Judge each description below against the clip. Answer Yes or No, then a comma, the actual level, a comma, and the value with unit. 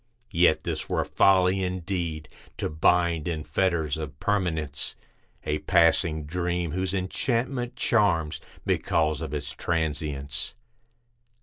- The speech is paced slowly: Yes, slow, 110 wpm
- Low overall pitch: Yes, very low, 85 Hz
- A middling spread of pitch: Yes, average, 3.4 semitones